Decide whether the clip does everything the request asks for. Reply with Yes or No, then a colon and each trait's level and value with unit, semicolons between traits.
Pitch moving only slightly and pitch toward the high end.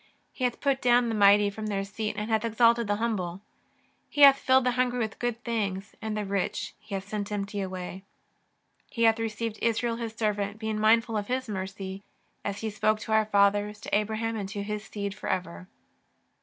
Yes: narrow, 2.2 semitones; high, 215 Hz